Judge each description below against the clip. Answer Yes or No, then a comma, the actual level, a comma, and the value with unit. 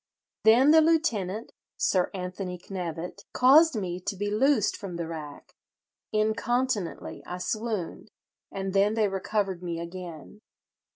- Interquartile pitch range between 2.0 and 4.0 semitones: Yes, average, 3.6 semitones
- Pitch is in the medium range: No, high, 195 Hz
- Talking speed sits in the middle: No, slow, 125 wpm